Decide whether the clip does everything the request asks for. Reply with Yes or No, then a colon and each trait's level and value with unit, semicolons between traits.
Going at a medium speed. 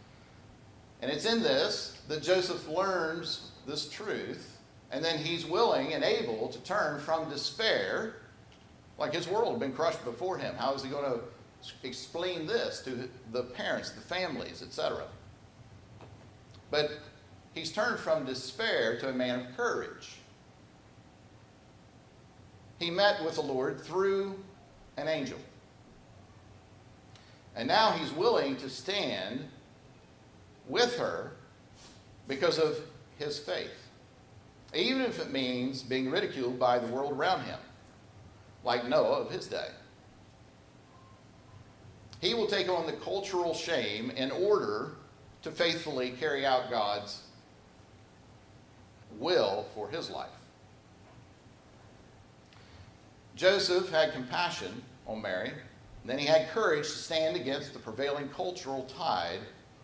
No: slow, 120 wpm